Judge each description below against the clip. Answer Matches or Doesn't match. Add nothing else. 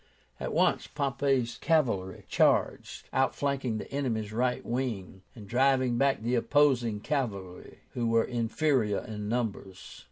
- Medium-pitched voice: Doesn't match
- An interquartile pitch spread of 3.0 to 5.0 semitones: Matches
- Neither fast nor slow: Doesn't match